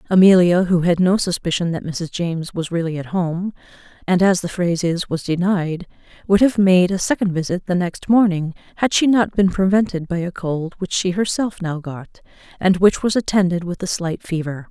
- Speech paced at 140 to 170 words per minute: No, average, 200 wpm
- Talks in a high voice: No, medium, 180 Hz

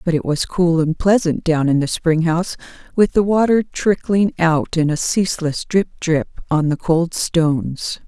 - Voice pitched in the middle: Yes, medium, 165 Hz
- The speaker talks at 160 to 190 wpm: Yes, average, 185 wpm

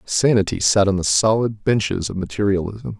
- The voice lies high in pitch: No, low, 100 Hz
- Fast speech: No, average, 160 wpm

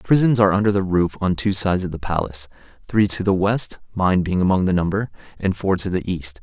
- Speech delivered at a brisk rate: Yes, fast, 245 wpm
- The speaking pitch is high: No, very low, 95 Hz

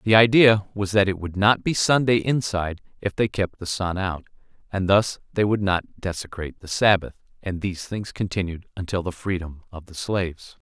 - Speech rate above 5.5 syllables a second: No, 5.2 syllables/s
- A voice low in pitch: Yes, very low, 95 Hz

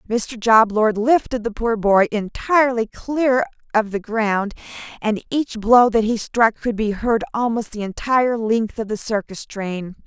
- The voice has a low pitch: No, high, 225 Hz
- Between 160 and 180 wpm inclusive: Yes, average, 175 wpm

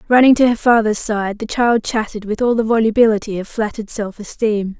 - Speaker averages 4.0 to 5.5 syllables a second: No, 5.9 syllables/s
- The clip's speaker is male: No, female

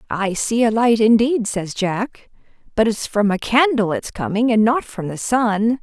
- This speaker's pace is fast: No, average, 195 wpm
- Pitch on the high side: Yes, high, 220 Hz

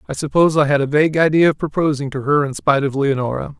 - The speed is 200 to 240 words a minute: No, fast, 250 wpm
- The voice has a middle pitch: Yes, medium, 145 Hz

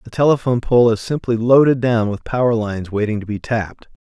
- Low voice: Yes, low, 115 Hz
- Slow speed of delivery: No, fast, 205 wpm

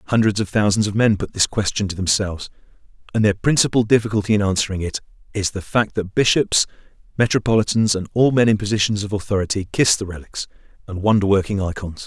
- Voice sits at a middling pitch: No, low, 105 Hz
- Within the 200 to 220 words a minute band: No, average, 185 wpm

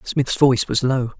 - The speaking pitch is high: No, low, 130 Hz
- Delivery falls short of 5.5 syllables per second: Yes, 4.7 syllables/s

